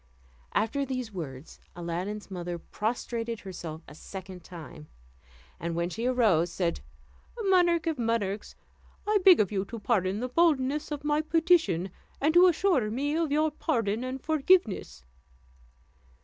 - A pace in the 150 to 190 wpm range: No, average, 140 wpm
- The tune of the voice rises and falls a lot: Yes, wide, 8.5 semitones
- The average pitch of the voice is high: Yes, high, 230 Hz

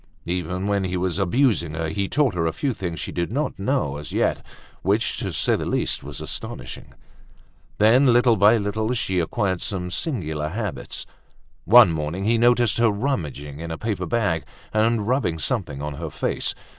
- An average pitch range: No, wide, 5.9 semitones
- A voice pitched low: Yes, low, 100 Hz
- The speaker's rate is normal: Yes, average, 180 wpm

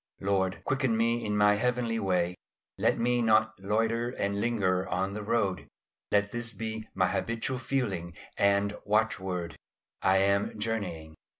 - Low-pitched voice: Yes, low, 105 Hz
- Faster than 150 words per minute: No, average, 140 wpm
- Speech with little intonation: No, average, 3.1 semitones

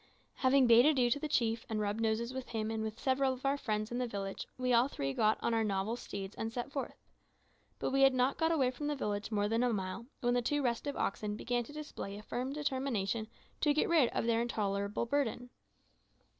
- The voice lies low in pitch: No, high, 235 Hz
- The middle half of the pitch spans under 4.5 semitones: Yes, average, 3.6 semitones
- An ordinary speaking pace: No, fast, 225 wpm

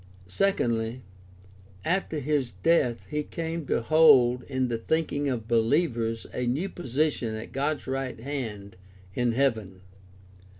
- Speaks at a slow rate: Yes, slow, 125 wpm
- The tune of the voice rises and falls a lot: No, average, 4.8 semitones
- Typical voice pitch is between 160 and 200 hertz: No, low, 130 Hz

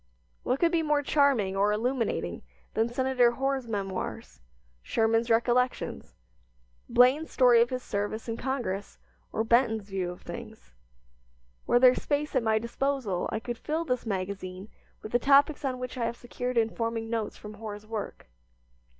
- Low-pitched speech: No, high, 235 Hz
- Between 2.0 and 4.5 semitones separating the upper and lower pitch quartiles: Yes, average, 3.3 semitones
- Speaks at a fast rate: No, average, 155 wpm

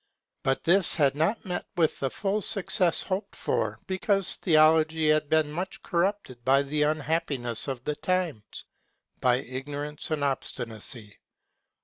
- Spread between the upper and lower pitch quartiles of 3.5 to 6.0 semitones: Yes, average, 4.7 semitones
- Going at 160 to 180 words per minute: No, slow, 135 wpm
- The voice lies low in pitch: No, medium, 155 Hz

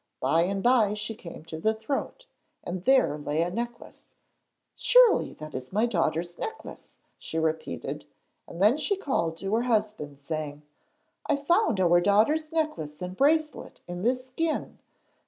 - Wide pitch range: Yes, wide, 8.0 semitones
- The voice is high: Yes, high, 205 Hz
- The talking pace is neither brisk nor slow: Yes, average, 155 wpm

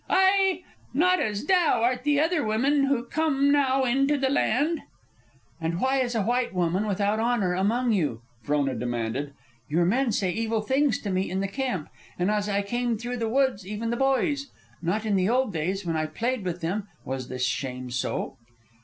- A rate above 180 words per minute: Yes, average, 190 wpm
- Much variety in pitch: Yes, wide, 6.8 semitones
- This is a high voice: Yes, high, 220 Hz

